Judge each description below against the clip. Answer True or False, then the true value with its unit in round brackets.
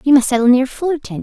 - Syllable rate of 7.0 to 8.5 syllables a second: True (7.1 syllables/s)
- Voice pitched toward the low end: False (265 Hz)